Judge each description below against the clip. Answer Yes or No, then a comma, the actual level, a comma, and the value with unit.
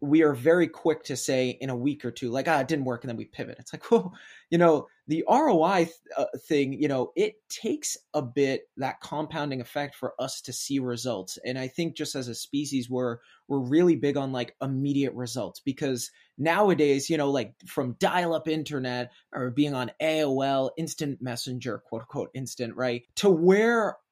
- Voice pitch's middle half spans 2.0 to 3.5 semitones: No, average, 4.1 semitones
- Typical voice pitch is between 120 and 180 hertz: Yes, medium, 140 Hz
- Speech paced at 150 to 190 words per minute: No, average, 200 wpm